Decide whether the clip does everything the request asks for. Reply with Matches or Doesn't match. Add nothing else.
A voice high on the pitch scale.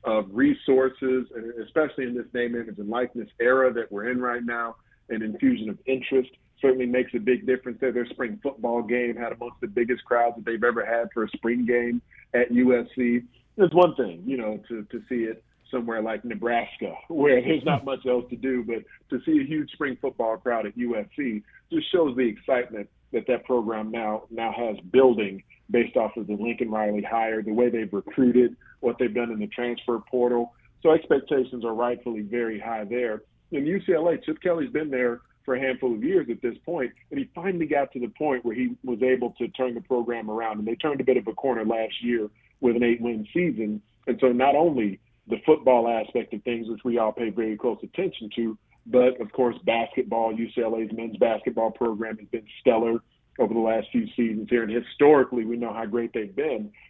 Doesn't match